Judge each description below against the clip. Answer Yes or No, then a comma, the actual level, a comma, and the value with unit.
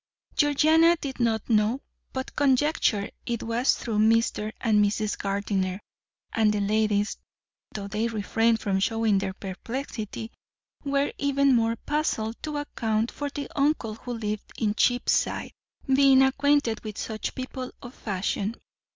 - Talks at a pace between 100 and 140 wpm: Yes, slow, 135 wpm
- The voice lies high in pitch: Yes, high, 225 Hz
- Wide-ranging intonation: No, average, 4.1 semitones